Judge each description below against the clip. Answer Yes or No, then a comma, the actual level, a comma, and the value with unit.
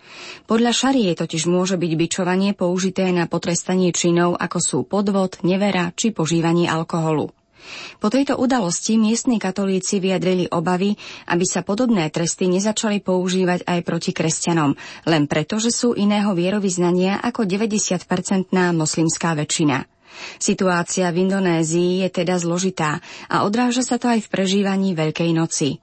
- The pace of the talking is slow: No, average, 135 wpm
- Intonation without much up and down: No, average, 3.0 semitones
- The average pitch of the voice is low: No, medium, 185 Hz